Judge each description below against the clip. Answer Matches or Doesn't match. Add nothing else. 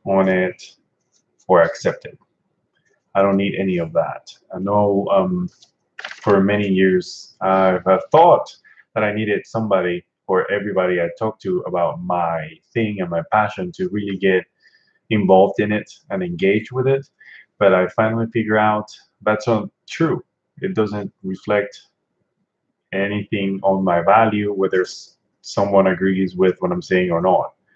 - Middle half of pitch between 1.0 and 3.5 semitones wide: Matches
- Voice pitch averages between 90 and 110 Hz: Matches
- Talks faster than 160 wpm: Doesn't match